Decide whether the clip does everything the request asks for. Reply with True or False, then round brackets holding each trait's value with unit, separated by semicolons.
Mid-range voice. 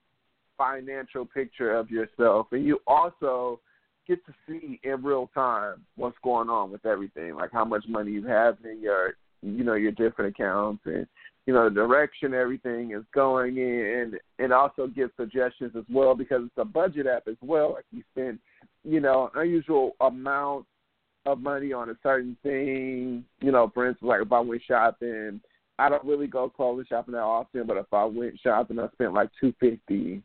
False (125 Hz)